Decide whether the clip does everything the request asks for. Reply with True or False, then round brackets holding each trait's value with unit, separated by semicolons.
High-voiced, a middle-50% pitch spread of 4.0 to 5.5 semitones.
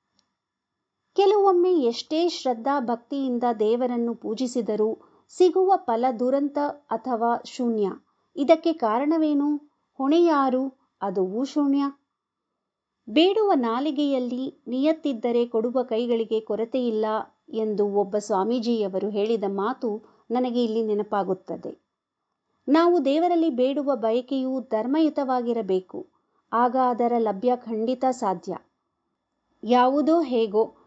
True (250 Hz; 4.5 semitones)